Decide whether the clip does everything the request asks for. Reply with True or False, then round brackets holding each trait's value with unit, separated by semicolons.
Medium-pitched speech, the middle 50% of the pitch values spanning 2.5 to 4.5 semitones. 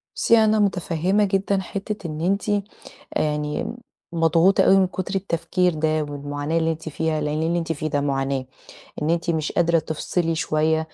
True (165 Hz; 3.2 semitones)